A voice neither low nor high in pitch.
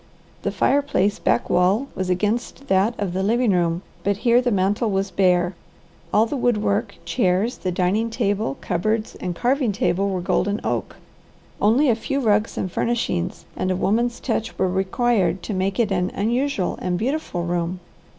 No: high, 200 Hz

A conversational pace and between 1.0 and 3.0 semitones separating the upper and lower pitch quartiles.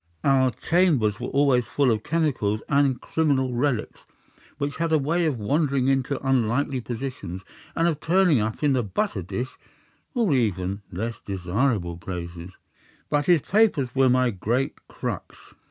No: average, 155 wpm; average, 5.3 semitones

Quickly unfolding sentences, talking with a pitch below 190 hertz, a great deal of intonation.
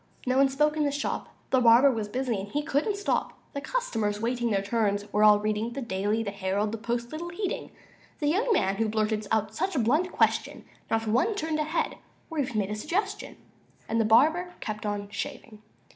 No: fast, 210 wpm; high, 235 Hz; wide, 6.1 semitones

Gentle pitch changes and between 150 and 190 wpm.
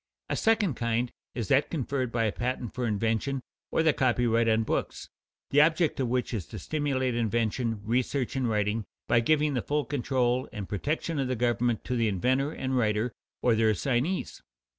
No: average, 3.2 semitones; average, 185 wpm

